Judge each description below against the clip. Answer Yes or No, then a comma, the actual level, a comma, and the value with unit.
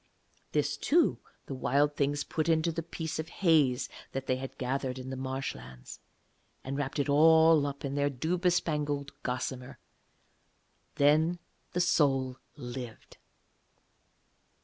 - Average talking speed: No, slow, 130 wpm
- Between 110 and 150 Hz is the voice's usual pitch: Yes, medium, 140 Hz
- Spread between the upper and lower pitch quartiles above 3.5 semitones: No, average, 3.2 semitones